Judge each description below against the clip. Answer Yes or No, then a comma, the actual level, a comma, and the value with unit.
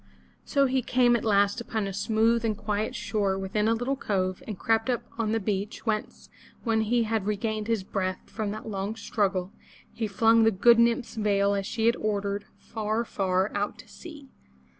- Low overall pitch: No, high, 215 Hz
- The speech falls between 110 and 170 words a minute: No, average, 195 wpm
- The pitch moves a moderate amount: No, narrow, 2.2 semitones